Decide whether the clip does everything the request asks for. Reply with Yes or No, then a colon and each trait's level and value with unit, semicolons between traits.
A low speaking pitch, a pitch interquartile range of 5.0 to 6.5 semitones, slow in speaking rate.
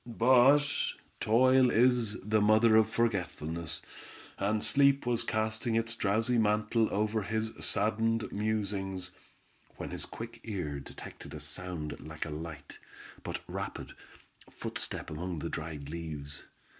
Yes: low, 105 Hz; average, 5.3 semitones; slow, 125 wpm